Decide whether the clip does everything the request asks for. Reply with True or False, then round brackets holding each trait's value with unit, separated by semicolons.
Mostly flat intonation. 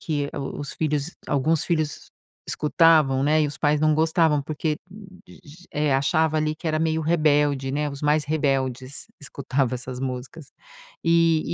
True (2.2 semitones)